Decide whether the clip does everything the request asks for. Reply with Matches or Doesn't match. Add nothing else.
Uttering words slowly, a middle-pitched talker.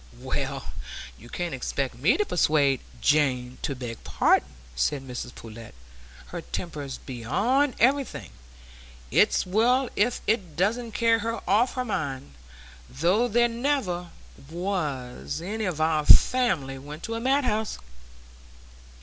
Matches